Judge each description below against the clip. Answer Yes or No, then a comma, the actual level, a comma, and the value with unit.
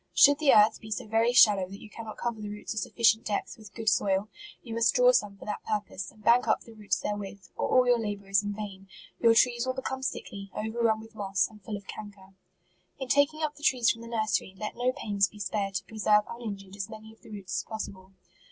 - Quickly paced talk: Yes, fast, 250 wpm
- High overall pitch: Yes, high, 215 Hz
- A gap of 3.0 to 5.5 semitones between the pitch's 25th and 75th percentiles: No, narrow, 2.6 semitones